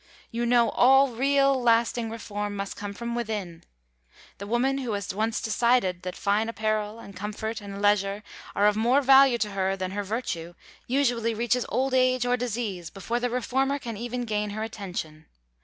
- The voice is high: Yes, high, 225 Hz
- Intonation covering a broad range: No, average, 3.3 semitones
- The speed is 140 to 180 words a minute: Yes, average, 175 wpm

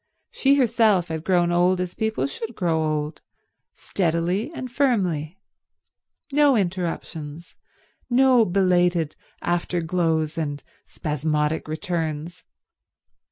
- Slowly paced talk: Yes, slow, 95 wpm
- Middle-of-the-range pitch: Yes, medium, 175 Hz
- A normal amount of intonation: Yes, average, 4.1 semitones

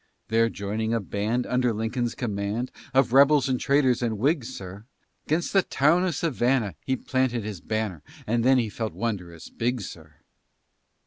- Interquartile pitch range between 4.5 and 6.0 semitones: No, average, 3.6 semitones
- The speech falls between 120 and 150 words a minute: No, average, 165 wpm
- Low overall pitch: Yes, low, 115 Hz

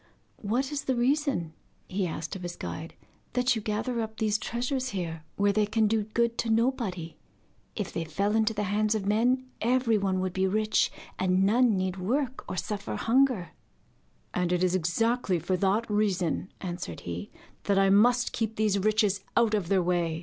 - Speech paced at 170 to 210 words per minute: Yes, average, 180 wpm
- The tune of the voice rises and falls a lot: No, average, 3.9 semitones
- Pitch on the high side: Yes, high, 210 Hz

